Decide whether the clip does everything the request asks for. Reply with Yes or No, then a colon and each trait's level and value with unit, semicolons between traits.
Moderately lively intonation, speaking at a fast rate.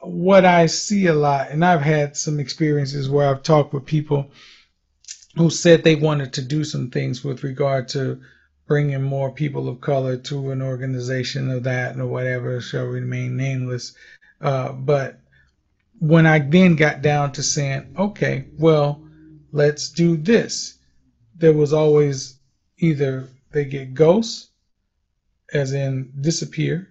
No: average, 3.0 semitones; average, 145 wpm